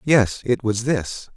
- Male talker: Yes, male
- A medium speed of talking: Yes, average, 175 wpm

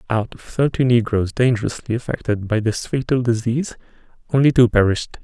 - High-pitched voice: No, low, 120 Hz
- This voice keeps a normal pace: Yes, average, 150 wpm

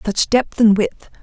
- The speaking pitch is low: No, high, 220 Hz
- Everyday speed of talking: Yes, average, 195 wpm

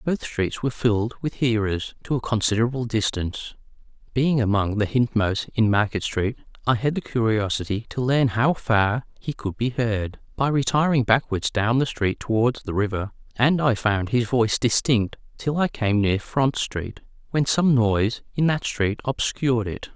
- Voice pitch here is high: No, low, 115 Hz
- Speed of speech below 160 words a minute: No, average, 175 wpm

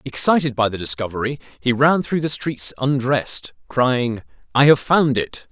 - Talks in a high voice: No, low, 125 Hz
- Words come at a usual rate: Yes, average, 165 wpm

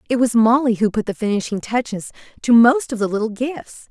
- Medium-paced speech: No, fast, 215 wpm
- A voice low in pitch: No, high, 230 Hz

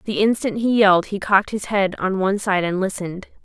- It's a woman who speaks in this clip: Yes, female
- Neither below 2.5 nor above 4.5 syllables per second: No, 6.0 syllables/s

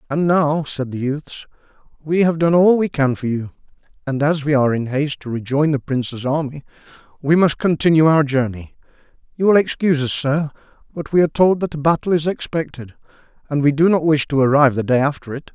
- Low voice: No, medium, 150 Hz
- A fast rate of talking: Yes, fast, 210 wpm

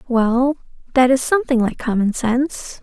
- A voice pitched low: No, very high, 250 Hz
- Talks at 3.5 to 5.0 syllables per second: Yes, 4.8 syllables/s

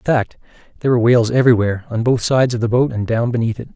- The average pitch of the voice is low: Yes, low, 120 Hz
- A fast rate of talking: Yes, fast, 255 wpm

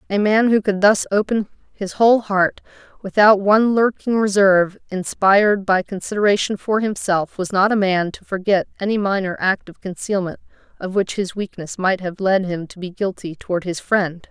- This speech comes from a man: No, female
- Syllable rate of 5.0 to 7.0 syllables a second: Yes, 5.1 syllables/s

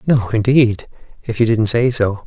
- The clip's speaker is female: No, male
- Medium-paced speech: Yes, average, 185 wpm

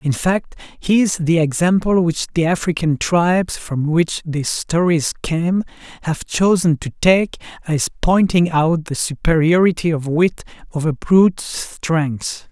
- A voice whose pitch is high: No, medium, 165 Hz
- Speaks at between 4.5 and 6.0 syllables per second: No, 4.0 syllables/s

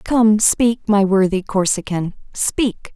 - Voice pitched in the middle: No, high, 210 Hz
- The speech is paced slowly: Yes, slow, 120 wpm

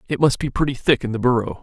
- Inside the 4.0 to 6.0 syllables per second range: No, 6.9 syllables/s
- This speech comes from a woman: No, male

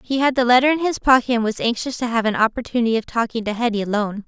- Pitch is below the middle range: No, high, 235 Hz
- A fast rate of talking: Yes, fast, 265 wpm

